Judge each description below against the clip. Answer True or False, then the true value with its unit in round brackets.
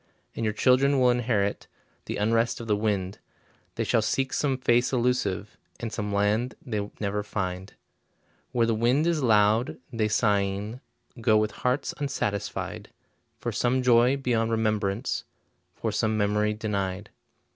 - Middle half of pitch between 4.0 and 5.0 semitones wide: False (3.1 semitones)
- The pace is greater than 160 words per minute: False (145 wpm)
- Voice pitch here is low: True (110 Hz)